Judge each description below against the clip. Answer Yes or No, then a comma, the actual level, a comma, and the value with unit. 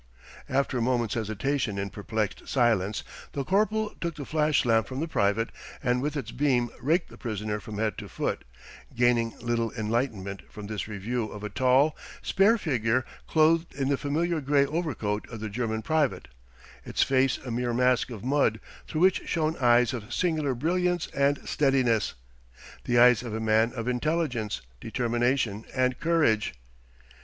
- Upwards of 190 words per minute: No, average, 165 wpm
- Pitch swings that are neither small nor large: Yes, average, 4.7 semitones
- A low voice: Yes, low, 125 Hz